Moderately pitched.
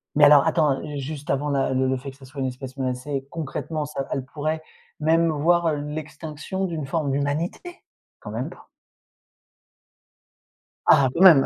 Yes: medium, 145 Hz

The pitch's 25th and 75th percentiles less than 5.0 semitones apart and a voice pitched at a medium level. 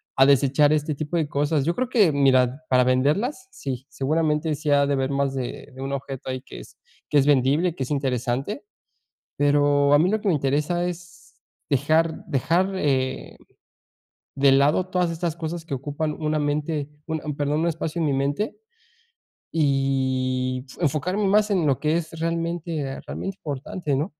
Yes: average, 3.4 semitones; medium, 145 Hz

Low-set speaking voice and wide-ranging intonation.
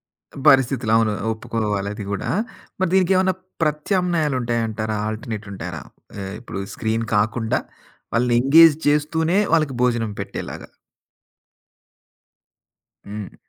Yes: low, 120 Hz; wide, 5.9 semitones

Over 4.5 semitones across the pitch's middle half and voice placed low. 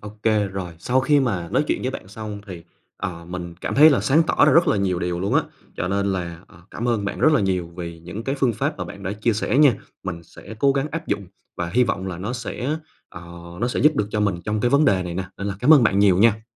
Yes: wide, 5.5 semitones; low, 105 Hz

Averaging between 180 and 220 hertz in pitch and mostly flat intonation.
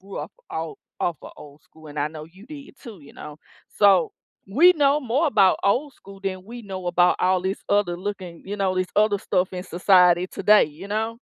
No: high, 190 Hz; average, 3.3 semitones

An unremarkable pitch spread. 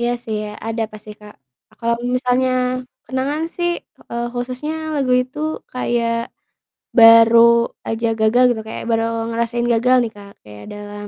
No: narrow, 2.3 semitones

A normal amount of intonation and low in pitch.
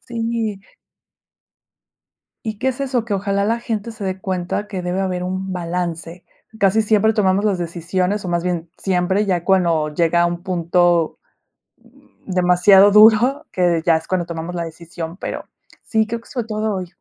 No: average, 3.4 semitones; medium, 185 Hz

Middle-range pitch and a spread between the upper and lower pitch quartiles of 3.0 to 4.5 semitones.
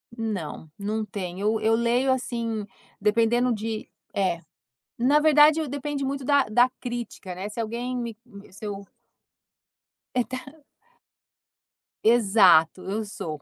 No: high, 225 Hz; average, 3.7 semitones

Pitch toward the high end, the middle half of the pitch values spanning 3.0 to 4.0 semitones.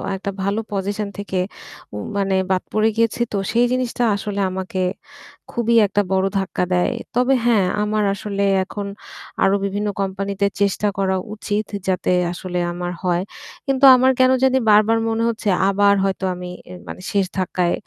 No: high, 200 Hz; narrow, 2.5 semitones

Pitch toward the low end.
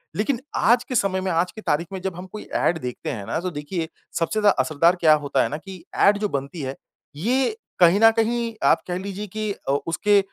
No: medium, 185 Hz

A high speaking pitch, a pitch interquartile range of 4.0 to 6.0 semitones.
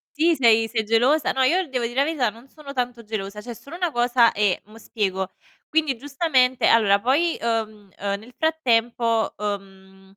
Yes: high, 235 Hz; average, 4.6 semitones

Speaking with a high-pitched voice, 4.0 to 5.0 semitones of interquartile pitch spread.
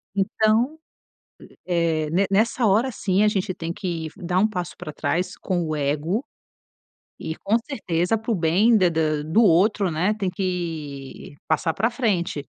No: medium, 180 Hz; average, 4.7 semitones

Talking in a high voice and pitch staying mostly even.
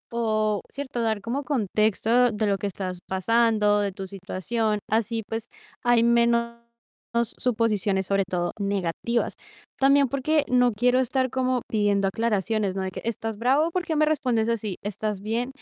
No: high, 225 Hz; average, 3.3 semitones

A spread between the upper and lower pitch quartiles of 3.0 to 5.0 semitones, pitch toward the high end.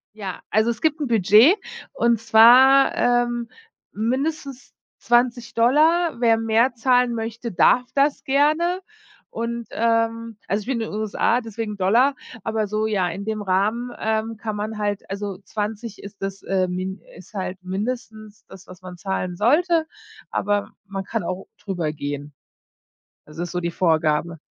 Yes: average, 3.7 semitones; high, 220 Hz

